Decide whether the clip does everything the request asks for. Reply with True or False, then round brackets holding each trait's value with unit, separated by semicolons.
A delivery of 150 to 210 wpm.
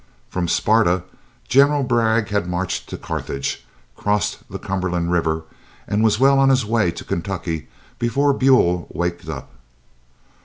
False (140 wpm)